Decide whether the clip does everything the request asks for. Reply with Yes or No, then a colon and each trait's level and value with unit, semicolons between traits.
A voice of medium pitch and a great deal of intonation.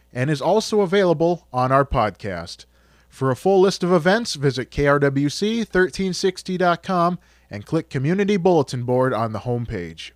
Yes: medium, 145 Hz; wide, 6.9 semitones